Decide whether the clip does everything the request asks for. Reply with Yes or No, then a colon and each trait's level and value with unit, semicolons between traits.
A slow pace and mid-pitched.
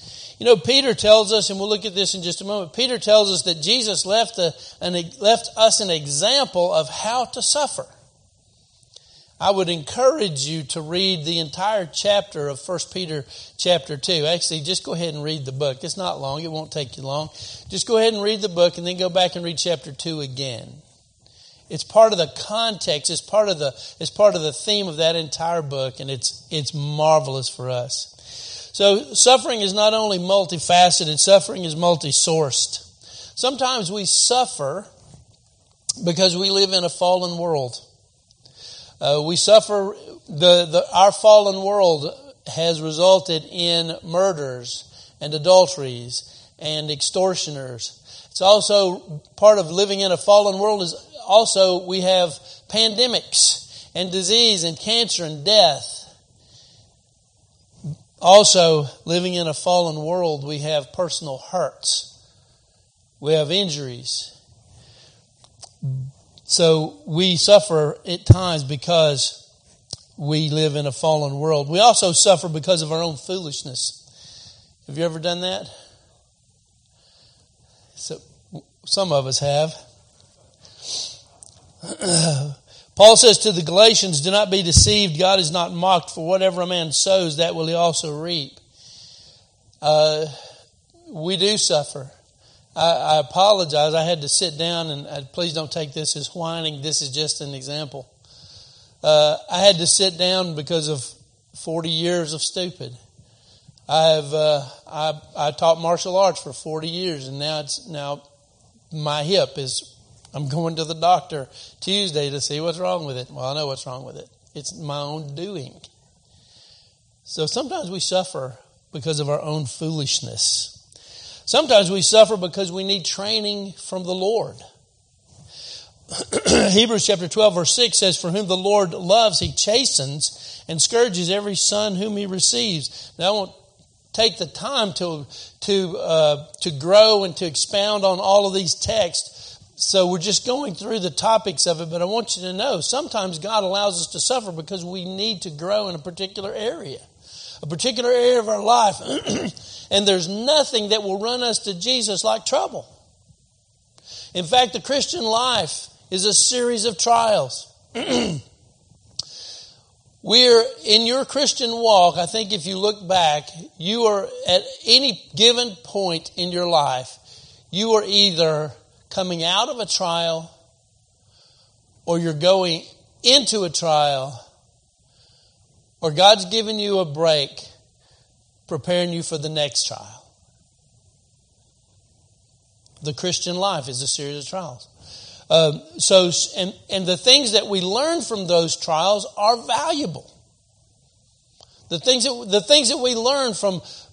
No: average, 150 wpm; medium, 165 Hz